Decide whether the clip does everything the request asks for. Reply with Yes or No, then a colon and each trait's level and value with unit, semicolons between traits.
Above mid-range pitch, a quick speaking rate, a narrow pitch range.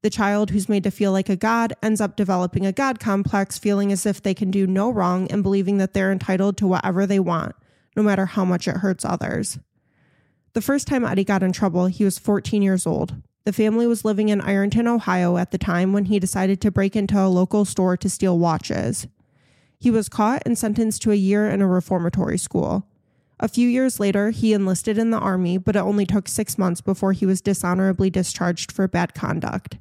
Yes: high, 195 Hz; fast, 215 wpm; narrow, 2.1 semitones